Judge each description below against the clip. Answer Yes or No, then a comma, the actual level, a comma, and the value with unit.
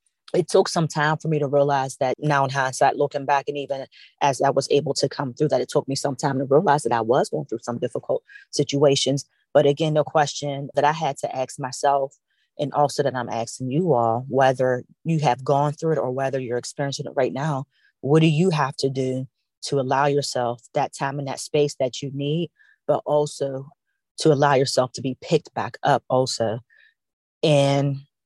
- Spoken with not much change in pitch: Yes, narrow, 1.9 semitones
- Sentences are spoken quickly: Yes, fast, 210 wpm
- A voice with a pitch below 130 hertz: No, medium, 140 Hz